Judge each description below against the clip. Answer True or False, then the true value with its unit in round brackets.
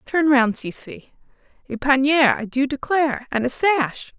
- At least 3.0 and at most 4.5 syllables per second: True (4.3 syllables/s)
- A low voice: False (270 Hz)